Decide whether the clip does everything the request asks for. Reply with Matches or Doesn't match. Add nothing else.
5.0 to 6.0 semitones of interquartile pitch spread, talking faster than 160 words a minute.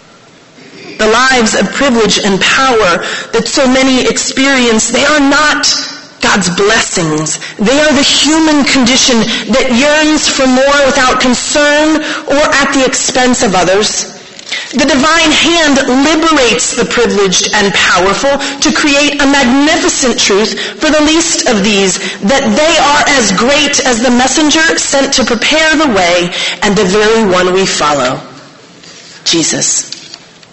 Doesn't match